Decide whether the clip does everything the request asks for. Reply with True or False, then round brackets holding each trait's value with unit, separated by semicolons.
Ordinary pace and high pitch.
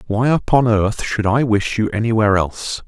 False (190 wpm; 110 Hz)